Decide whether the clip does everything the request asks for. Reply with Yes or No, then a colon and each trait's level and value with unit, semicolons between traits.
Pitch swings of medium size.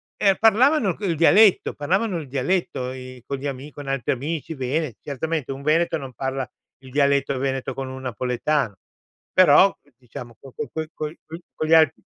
Yes: average, 3.8 semitones